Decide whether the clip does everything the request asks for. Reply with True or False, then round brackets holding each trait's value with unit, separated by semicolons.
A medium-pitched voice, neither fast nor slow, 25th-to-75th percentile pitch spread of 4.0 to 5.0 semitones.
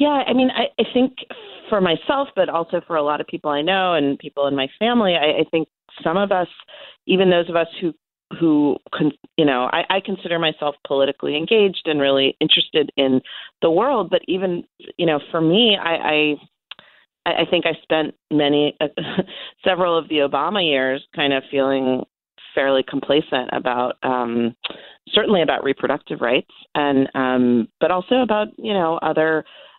True (160 Hz; 175 wpm; 4.7 semitones)